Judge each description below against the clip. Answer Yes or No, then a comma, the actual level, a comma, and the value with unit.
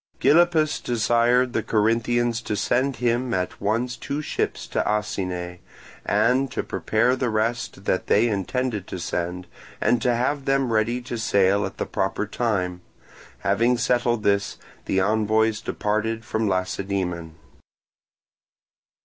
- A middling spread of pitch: Yes, average, 3.5 semitones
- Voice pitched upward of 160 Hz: No, low, 110 Hz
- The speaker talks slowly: Yes, slow, 130 wpm